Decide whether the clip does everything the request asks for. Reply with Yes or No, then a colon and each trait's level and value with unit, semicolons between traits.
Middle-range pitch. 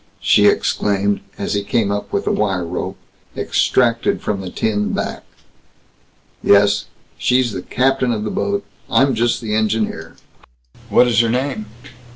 No: low, 110 Hz